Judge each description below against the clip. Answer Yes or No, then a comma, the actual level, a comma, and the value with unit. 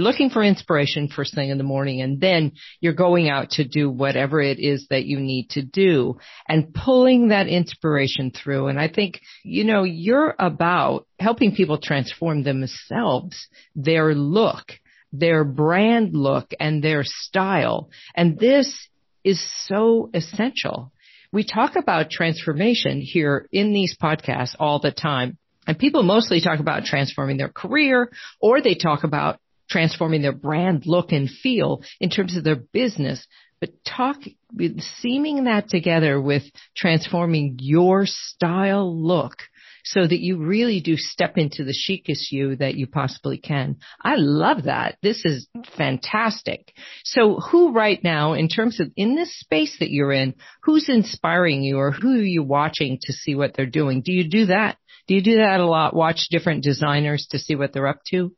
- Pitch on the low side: No, medium, 165 Hz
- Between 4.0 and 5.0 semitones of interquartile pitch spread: No, wide, 5.6 semitones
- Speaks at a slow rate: No, average, 165 wpm